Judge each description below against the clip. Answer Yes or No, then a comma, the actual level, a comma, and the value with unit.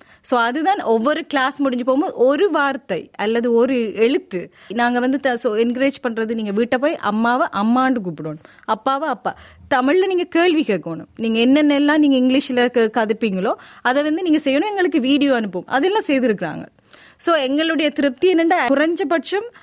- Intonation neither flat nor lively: Yes, average, 4.9 semitones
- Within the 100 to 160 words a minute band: Yes, average, 110 wpm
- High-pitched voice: Yes, very high, 265 Hz